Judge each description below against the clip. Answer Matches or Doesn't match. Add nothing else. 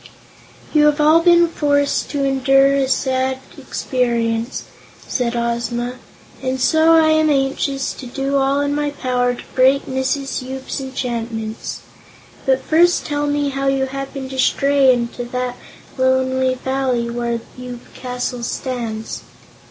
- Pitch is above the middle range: Matches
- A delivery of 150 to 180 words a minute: Doesn't match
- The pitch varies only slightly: Matches